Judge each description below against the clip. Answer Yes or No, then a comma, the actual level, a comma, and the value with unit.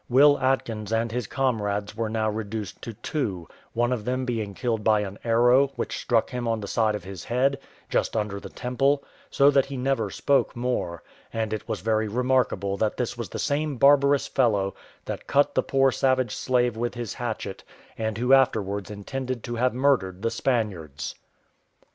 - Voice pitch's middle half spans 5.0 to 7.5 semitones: No, average, 3.5 semitones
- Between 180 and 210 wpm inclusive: Yes, average, 185 wpm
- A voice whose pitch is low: Yes, low, 115 Hz